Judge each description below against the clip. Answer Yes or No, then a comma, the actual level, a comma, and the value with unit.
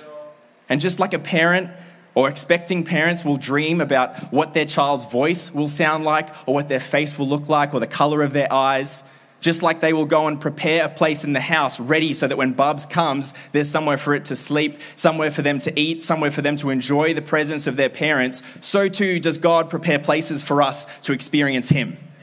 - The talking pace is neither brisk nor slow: No, fast, 220 wpm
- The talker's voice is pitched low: No, medium, 150 Hz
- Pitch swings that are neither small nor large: No, narrow, 2.3 semitones